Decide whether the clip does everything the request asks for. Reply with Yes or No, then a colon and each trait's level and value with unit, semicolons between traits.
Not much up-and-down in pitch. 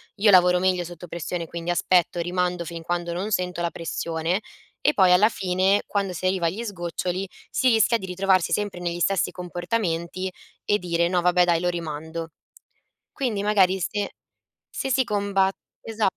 Yes: narrow, 2.3 semitones